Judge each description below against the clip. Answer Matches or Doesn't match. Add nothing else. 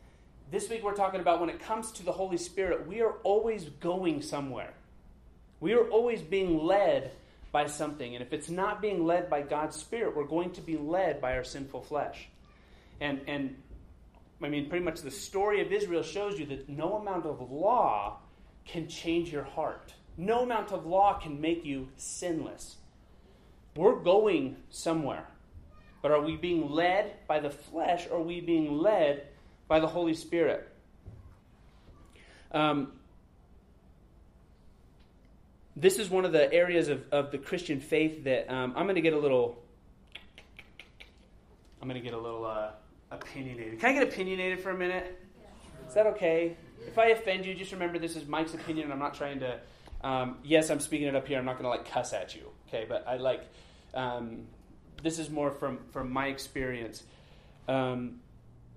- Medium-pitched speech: Matches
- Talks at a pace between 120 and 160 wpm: Doesn't match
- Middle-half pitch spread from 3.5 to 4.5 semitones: Doesn't match